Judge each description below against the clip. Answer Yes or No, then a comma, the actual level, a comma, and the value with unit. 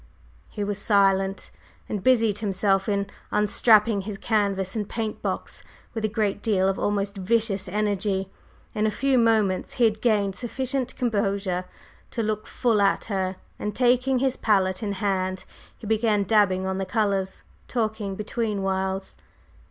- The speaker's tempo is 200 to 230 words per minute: No, average, 150 wpm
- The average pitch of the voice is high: Yes, high, 205 Hz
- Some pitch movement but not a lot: No, narrow, 2.3 semitones